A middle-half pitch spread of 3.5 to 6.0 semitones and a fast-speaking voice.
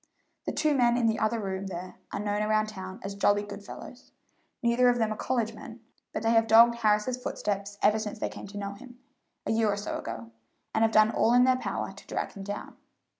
No: average, 2.7 semitones; fast, 230 wpm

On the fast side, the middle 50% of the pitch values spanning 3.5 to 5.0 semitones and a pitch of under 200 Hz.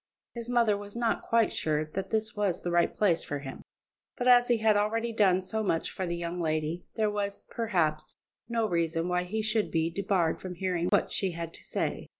Yes: fast, 210 wpm; average, 4.4 semitones; high, 190 Hz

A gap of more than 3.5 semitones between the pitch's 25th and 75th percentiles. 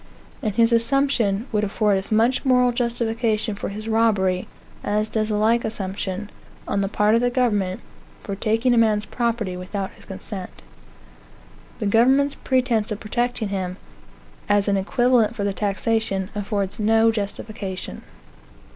No: average, 2.7 semitones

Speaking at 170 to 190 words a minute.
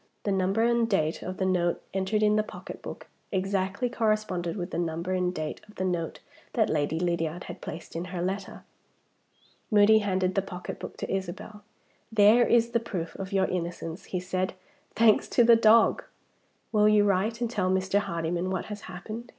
Yes: average, 180 wpm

